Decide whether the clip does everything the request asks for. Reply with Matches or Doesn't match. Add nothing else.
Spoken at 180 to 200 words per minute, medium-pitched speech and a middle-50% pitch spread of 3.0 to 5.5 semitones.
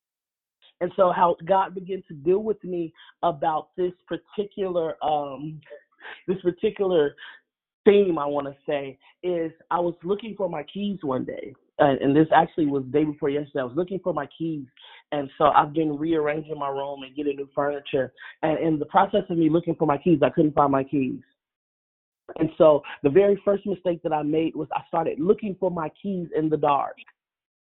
Matches